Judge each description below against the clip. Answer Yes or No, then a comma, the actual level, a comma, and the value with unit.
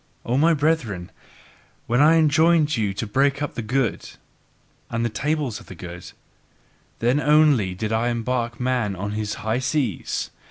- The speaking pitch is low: Yes, low, 120 Hz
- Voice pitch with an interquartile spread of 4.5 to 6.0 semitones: Yes, average, 5.3 semitones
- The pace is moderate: Yes, average, 160 wpm